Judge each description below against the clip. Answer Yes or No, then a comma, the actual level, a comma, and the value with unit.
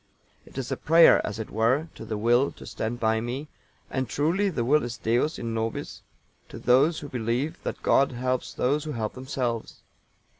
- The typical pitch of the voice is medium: No, low, 125 Hz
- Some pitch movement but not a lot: Yes, average, 4.0 semitones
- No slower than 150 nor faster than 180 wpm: No, average, 190 wpm